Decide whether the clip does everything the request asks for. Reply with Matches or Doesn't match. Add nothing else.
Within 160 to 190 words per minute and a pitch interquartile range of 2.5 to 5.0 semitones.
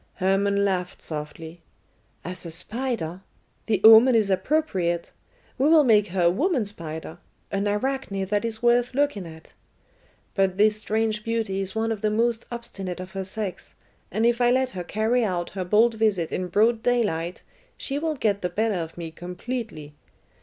Matches